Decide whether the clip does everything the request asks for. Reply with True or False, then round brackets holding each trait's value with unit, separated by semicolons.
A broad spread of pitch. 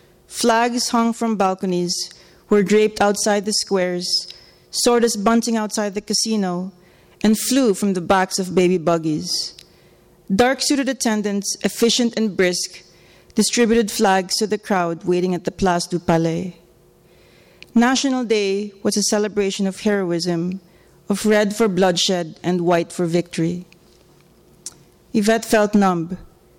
False (3.4 semitones)